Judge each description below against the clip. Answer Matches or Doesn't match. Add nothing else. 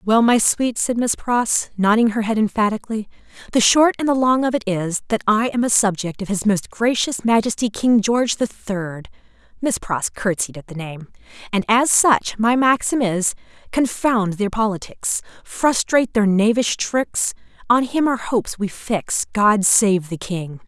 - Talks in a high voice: Matches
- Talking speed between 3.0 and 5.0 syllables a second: Matches